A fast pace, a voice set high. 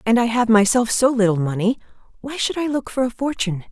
Yes: fast, 225 wpm; high, 230 Hz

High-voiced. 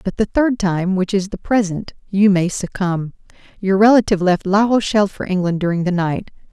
Yes: high, 195 Hz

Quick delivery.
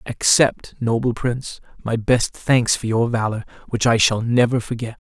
No: average, 165 wpm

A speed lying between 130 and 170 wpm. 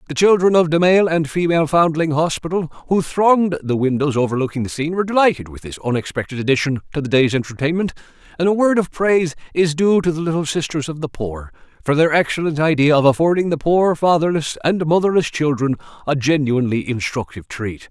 No: average, 190 wpm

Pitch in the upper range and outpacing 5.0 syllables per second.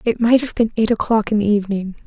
Yes: high, 215 Hz; 6.5 syllables/s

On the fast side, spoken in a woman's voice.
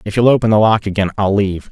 No: fast, 280 wpm; male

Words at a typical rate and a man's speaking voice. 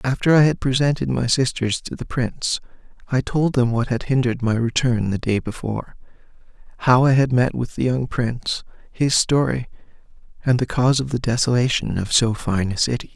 Yes: average, 185 wpm; male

